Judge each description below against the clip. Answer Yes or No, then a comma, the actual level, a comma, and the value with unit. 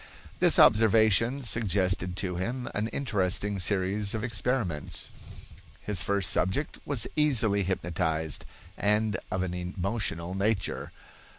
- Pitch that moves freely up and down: No, average, 3.4 semitones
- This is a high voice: No, low, 100 Hz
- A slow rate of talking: Yes, slow, 110 wpm